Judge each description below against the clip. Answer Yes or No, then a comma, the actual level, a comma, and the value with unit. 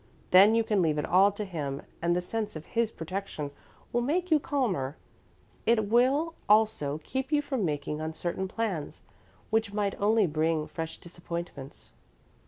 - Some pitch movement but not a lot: No, wide, 6.0 semitones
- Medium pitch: No, high, 195 Hz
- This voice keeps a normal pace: Yes, average, 160 wpm